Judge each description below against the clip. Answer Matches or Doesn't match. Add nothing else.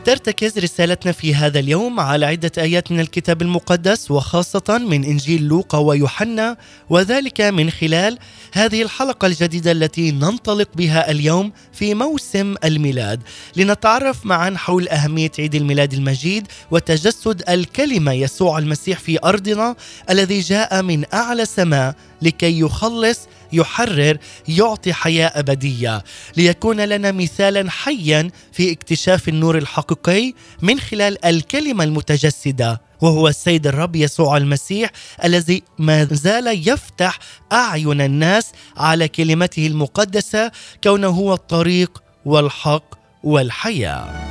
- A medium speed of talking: Matches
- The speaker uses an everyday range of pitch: Matches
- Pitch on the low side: Doesn't match